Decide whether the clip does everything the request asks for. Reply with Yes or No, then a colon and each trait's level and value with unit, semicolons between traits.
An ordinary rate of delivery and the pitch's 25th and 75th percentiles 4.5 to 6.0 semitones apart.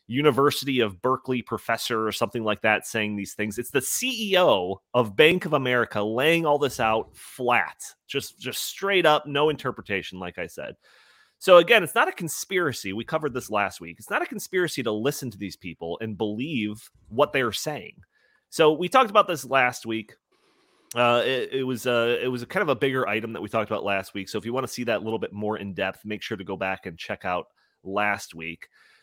No: fast, 220 wpm; average, 5.3 semitones